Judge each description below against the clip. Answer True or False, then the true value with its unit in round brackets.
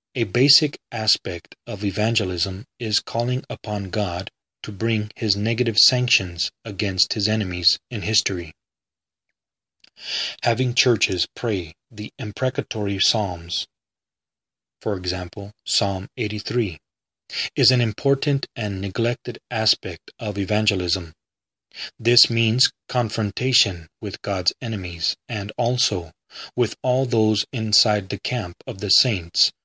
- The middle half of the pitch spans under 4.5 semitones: True (3.7 semitones)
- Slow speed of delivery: True (110 wpm)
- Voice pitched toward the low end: True (105 Hz)